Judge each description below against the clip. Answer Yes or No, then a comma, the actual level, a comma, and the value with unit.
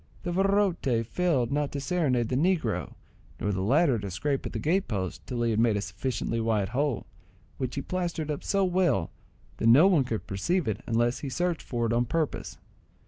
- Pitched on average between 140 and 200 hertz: No, low, 130 Hz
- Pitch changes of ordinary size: No, wide, 6.9 semitones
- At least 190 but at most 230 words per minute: Yes, average, 200 wpm